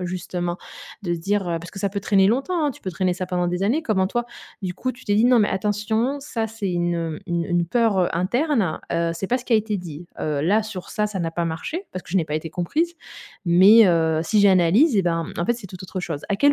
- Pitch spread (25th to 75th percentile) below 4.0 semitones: No, average, 4.3 semitones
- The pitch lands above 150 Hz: Yes, high, 190 Hz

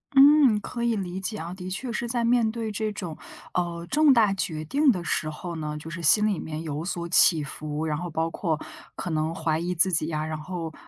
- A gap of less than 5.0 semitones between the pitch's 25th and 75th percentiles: No, average, 5.3 semitones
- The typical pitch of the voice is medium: Yes, medium, 175 Hz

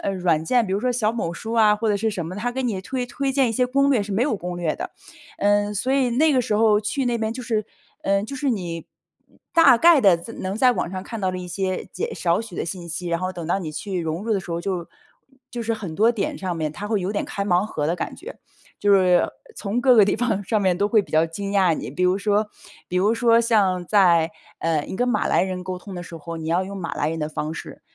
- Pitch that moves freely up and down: No, average, 4.3 semitones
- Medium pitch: No, high, 200 Hz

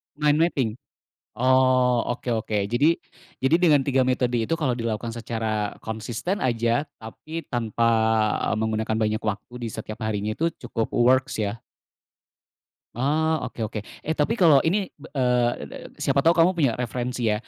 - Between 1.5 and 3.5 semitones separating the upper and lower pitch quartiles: No, average, 4.5 semitones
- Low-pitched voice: Yes, low, 125 Hz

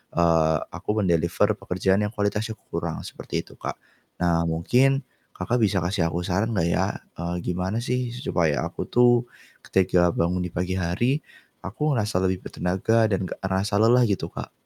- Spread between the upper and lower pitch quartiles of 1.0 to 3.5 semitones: No, average, 4.2 semitones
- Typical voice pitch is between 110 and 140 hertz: No, very low, 95 Hz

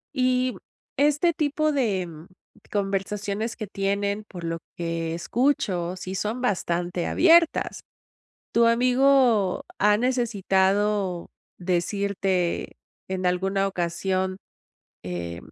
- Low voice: No, high, 200 Hz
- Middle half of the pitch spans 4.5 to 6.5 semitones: Yes, average, 4.9 semitones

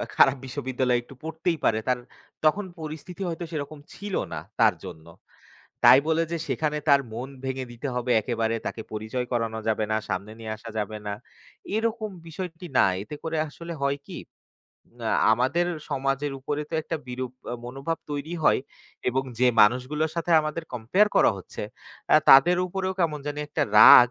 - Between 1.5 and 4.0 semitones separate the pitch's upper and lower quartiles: No, average, 4.8 semitones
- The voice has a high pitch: No, medium, 140 Hz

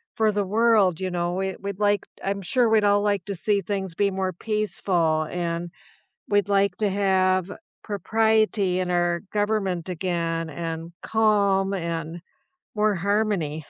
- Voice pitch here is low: No, high, 195 Hz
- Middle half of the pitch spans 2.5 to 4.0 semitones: Yes, average, 2.9 semitones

